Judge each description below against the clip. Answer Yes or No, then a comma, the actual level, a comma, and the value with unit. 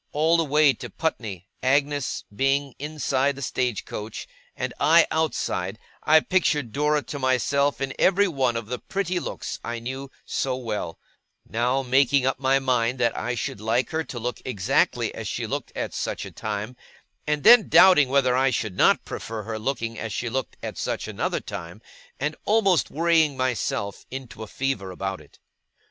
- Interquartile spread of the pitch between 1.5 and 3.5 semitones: No, average, 4.2 semitones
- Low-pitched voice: Yes, low, 130 Hz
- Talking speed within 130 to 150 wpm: No, average, 175 wpm